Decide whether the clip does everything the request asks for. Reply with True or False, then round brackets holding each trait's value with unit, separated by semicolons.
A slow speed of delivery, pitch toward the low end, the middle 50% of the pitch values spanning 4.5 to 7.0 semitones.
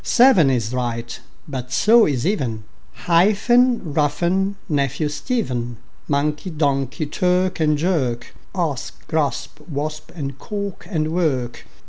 False (115 wpm; 150 Hz; 5.4 semitones)